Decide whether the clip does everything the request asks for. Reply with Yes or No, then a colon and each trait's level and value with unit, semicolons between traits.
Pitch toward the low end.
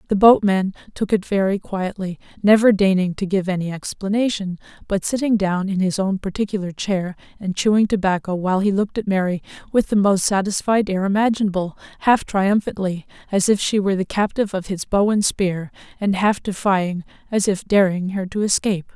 No: high, 195 Hz